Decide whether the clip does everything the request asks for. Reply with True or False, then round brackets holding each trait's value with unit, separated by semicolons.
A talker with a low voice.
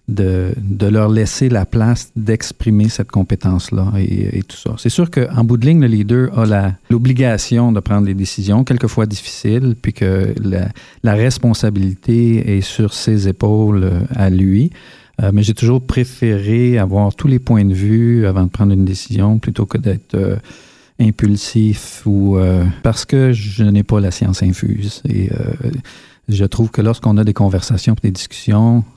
True (110 Hz)